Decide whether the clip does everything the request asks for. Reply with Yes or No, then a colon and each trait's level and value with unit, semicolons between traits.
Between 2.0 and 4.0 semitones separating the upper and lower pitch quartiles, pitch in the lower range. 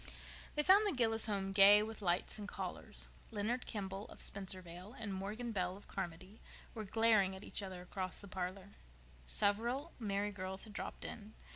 No: average, 2.7 semitones; high, 200 Hz